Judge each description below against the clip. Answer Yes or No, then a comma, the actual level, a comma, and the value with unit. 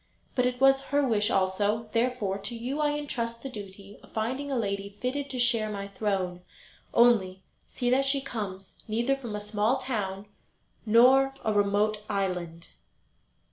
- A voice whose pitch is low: No, high, 220 Hz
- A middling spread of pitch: Yes, average, 4.3 semitones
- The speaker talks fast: No, average, 160 wpm